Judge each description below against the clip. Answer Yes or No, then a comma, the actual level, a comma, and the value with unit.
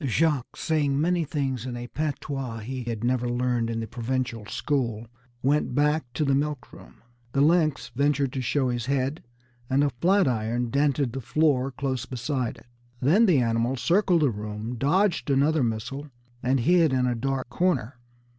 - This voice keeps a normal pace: Yes, average, 175 wpm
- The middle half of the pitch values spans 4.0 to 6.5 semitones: No, average, 3.4 semitones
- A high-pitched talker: No, low, 135 Hz